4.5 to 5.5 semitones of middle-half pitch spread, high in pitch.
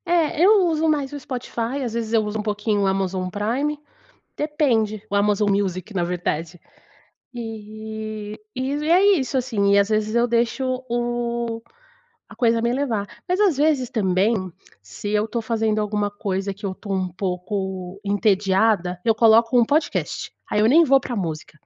No: average, 3.8 semitones; high, 220 Hz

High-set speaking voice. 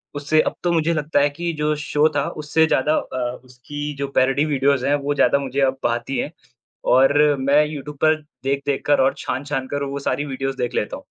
No: medium, 140 Hz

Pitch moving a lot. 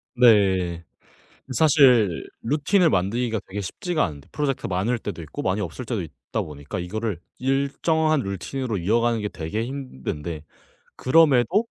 Yes: wide, 6.8 semitones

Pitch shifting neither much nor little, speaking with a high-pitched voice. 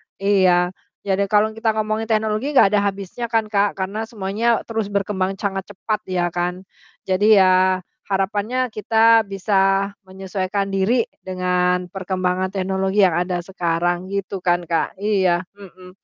No: narrow, 2.3 semitones; high, 195 Hz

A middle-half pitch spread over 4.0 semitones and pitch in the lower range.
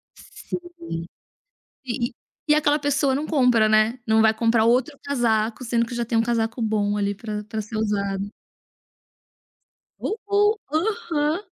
No: average, 4.6 semitones; high, 235 Hz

